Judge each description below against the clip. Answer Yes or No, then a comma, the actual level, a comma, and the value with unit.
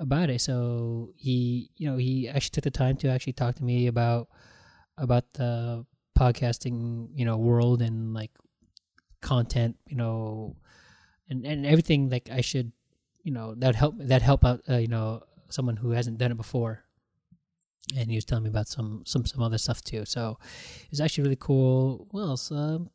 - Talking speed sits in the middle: Yes, average, 185 wpm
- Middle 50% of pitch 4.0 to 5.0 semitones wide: No, average, 2.7 semitones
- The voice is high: No, low, 125 Hz